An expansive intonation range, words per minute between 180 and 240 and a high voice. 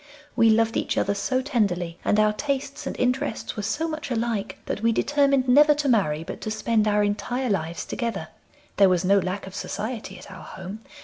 No: average, 4.5 semitones; average, 200 wpm; high, 215 Hz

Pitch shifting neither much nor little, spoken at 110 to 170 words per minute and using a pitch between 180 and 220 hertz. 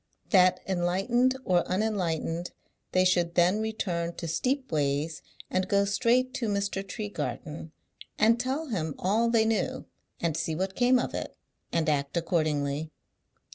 Yes: average, 5.0 semitones; slow, 135 wpm; medium, 185 Hz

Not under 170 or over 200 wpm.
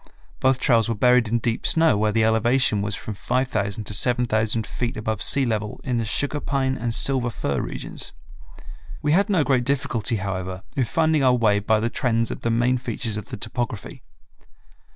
Yes: average, 190 wpm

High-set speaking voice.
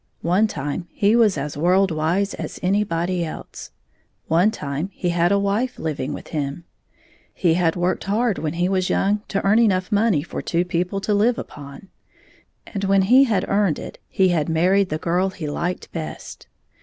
No: medium, 180 Hz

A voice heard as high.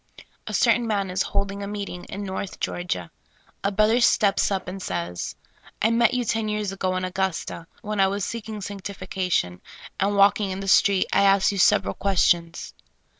Yes: high, 195 Hz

